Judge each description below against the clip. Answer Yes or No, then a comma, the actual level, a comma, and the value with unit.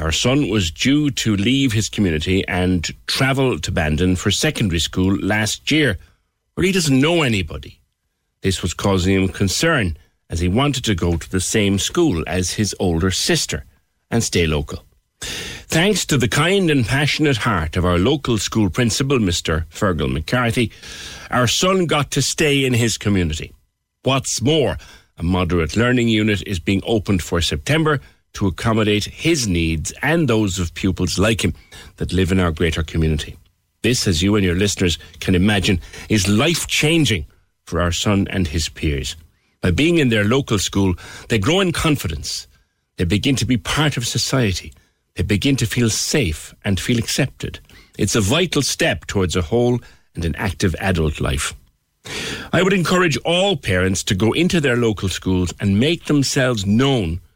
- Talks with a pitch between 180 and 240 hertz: No, low, 100 Hz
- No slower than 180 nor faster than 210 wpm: No, average, 170 wpm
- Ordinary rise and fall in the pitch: No, wide, 5.9 semitones